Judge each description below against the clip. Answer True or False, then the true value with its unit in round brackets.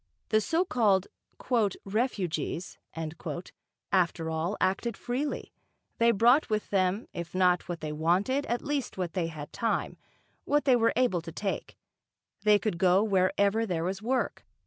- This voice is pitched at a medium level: False (200 Hz)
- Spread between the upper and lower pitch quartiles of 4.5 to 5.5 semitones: True (4.8 semitones)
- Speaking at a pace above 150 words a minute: False (145 wpm)